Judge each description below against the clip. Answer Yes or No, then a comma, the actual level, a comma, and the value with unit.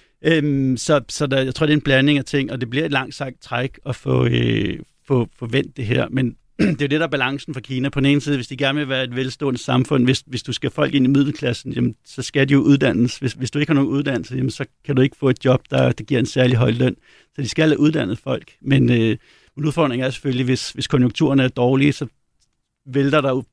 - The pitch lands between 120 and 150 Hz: Yes, low, 135 Hz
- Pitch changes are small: Yes, narrow, 2.2 semitones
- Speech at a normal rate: No, fast, 270 wpm